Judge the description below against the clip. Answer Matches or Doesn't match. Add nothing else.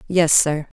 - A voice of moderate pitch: Matches